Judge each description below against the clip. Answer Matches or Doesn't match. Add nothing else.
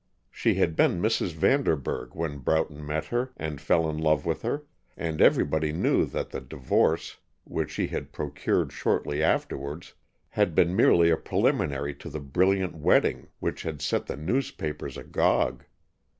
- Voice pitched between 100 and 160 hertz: Doesn't match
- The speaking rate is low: Doesn't match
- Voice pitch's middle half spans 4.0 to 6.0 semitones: Doesn't match